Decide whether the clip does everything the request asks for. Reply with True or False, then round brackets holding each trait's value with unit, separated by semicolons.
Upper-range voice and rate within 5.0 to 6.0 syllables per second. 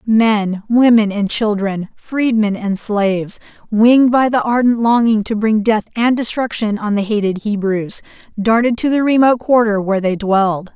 False (220 Hz; 4.6 syllables/s)